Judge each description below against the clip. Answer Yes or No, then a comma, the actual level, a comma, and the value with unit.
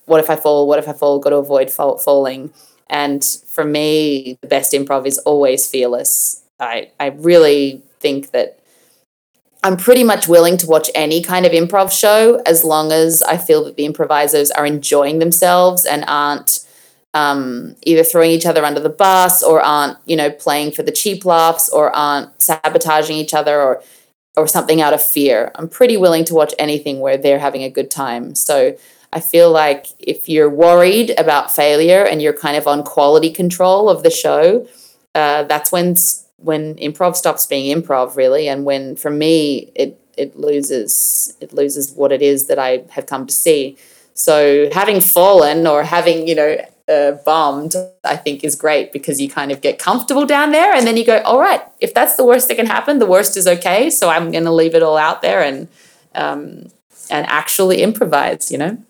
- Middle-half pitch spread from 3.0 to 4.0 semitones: Yes, average, 3.6 semitones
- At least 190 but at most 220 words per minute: Yes, average, 195 wpm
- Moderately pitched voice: Yes, medium, 155 Hz